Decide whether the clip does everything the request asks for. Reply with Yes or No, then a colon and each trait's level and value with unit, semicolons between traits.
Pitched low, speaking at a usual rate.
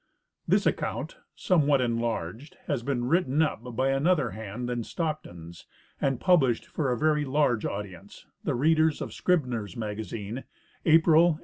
Yes: low, 130 Hz; average, 150 wpm